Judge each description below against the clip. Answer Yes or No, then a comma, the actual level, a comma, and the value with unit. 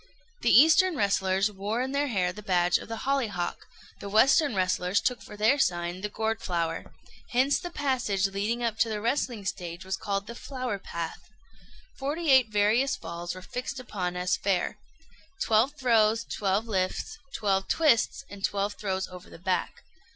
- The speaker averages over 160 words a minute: Yes, average, 170 wpm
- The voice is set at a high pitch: Yes, high, 210 Hz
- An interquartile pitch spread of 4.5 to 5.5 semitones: Yes, average, 5.0 semitones